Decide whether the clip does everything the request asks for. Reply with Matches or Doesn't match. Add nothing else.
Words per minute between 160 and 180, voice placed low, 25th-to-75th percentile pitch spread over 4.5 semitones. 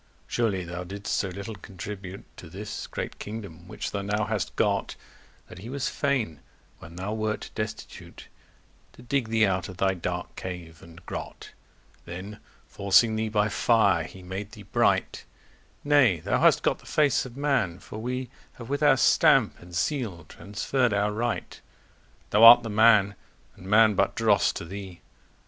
Doesn't match